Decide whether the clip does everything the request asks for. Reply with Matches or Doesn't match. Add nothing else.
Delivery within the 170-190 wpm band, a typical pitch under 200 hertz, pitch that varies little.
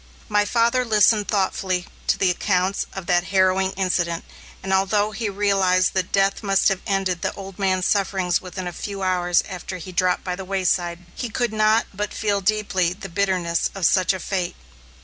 Matches